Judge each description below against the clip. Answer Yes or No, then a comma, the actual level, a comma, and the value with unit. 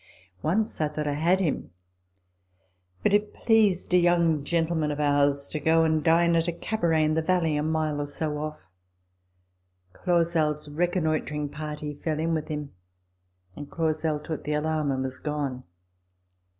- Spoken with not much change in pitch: Yes, narrow, 2.1 semitones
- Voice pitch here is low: No, medium, 155 Hz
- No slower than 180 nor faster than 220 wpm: No, average, 160 wpm